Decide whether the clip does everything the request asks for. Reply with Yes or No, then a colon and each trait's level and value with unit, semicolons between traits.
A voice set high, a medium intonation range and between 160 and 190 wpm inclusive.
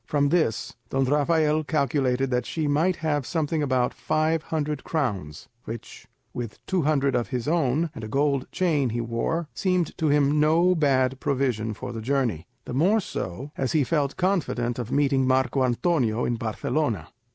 No: medium, 140 Hz; average, 4.2 semitones; average, 170 wpm